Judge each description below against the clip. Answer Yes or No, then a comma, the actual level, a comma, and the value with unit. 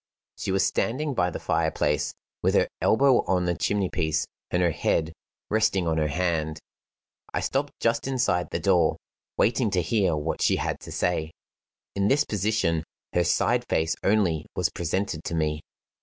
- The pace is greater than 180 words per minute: No, average, 170 wpm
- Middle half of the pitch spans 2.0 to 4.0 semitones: No, average, 5.1 semitones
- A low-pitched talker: Yes, very low, 90 Hz